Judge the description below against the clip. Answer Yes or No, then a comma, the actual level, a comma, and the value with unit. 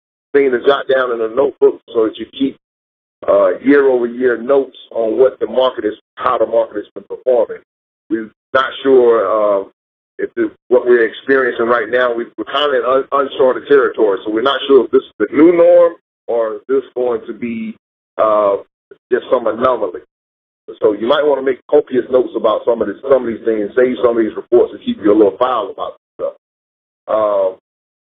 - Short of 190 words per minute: No, average, 200 wpm